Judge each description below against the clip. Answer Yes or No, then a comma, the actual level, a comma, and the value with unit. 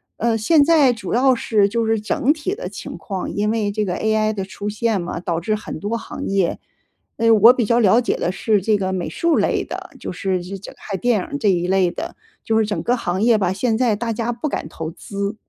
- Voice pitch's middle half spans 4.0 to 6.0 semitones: No, average, 3.3 semitones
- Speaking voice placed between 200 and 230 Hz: Yes, high, 215 Hz